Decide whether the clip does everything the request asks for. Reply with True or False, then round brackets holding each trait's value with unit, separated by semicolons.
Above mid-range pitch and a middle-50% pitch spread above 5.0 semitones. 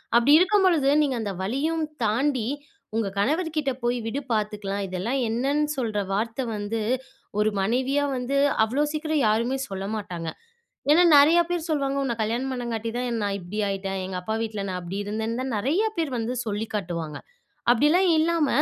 True (235 Hz; 5.6 semitones)